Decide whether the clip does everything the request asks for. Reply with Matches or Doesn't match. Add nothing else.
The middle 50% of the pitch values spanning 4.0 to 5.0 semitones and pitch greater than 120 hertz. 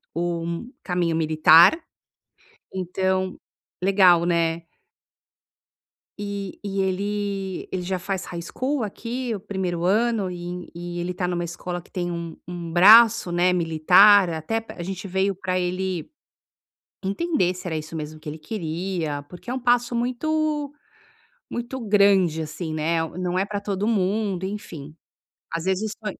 Doesn't match